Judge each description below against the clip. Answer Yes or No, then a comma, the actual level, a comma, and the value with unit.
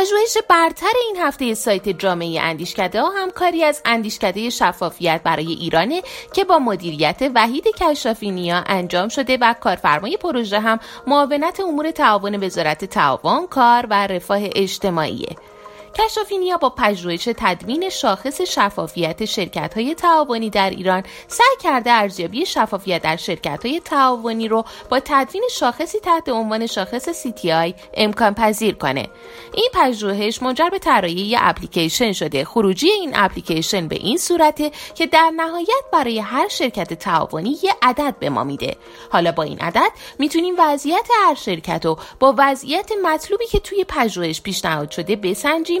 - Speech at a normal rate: Yes, average, 140 wpm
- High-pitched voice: Yes, high, 240 Hz